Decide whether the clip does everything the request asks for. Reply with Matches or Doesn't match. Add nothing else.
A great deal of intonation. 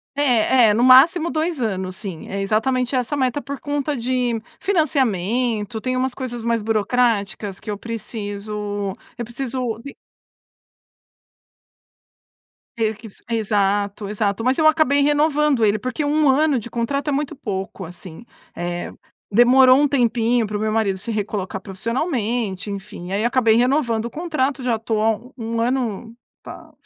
Doesn't match